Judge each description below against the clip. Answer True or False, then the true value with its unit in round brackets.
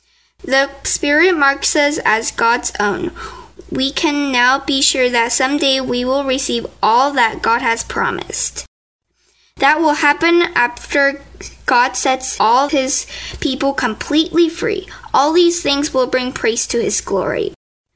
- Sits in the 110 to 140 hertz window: False (290 Hz)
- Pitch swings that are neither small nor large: True (4.8 semitones)